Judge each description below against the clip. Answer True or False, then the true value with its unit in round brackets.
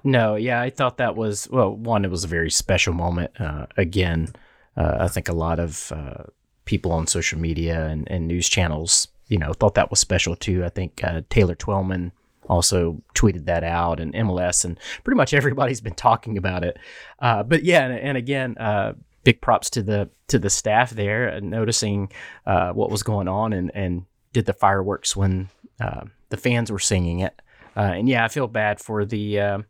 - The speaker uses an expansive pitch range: False (4.4 semitones)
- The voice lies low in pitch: True (100 Hz)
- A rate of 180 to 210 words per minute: True (200 wpm)